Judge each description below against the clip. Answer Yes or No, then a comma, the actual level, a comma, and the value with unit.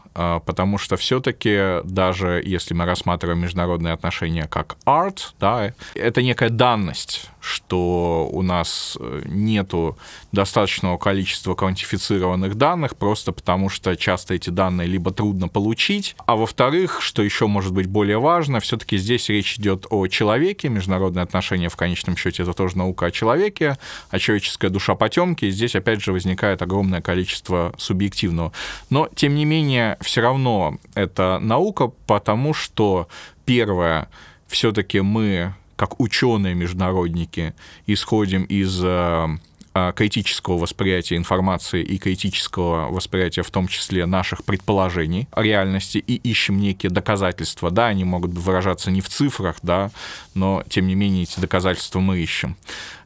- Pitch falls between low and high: No, very low, 95 Hz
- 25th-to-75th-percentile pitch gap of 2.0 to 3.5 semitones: Yes, average, 2.7 semitones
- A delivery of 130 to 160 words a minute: Yes, average, 135 wpm